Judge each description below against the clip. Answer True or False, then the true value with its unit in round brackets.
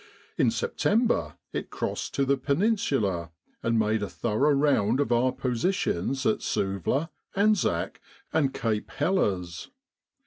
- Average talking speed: False (125 wpm)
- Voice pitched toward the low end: True (130 Hz)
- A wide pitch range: True (6.6 semitones)